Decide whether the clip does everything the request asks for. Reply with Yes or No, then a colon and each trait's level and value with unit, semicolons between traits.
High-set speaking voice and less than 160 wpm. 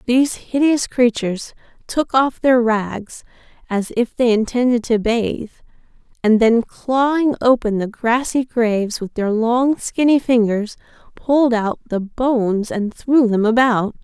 Yes: high, 235 Hz; average, 140 wpm